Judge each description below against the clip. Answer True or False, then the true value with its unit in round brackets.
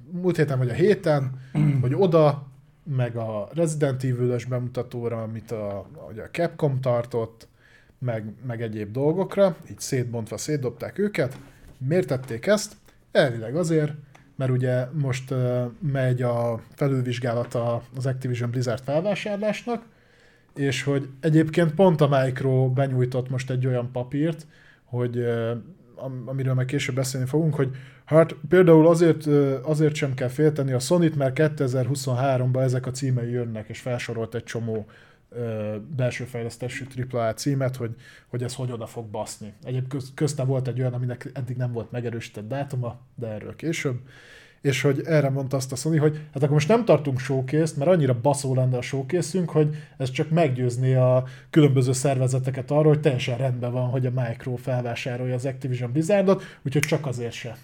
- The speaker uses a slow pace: False (155 wpm)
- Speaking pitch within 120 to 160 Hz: True (130 Hz)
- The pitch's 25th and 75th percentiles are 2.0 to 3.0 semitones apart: False (3.4 semitones)